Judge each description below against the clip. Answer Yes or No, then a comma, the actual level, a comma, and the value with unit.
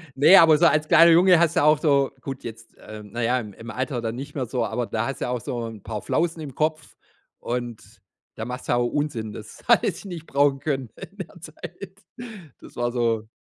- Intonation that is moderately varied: Yes, average, 5.0 semitones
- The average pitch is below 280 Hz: Yes, low, 135 Hz